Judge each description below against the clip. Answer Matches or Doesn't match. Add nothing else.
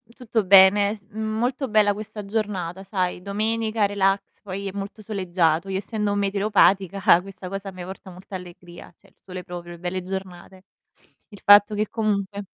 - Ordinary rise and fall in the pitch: Doesn't match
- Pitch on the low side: Doesn't match